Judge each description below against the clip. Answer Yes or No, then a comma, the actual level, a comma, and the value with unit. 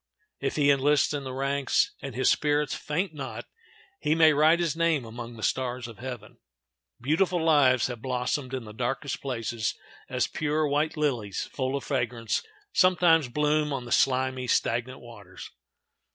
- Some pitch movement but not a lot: Yes, average, 3.4 semitones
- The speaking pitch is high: No, low, 135 Hz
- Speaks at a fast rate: No, average, 160 wpm